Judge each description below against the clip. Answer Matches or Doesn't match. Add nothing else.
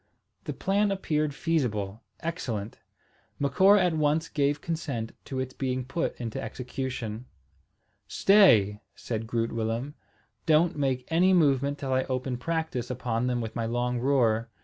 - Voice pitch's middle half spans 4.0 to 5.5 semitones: Matches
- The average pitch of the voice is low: Matches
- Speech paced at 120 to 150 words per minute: Matches